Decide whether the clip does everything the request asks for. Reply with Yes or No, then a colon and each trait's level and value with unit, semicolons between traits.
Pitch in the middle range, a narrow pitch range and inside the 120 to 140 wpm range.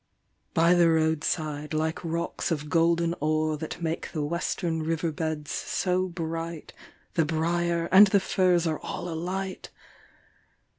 Yes: medium, 165 Hz; narrow, 1.6 semitones; slow, 135 wpm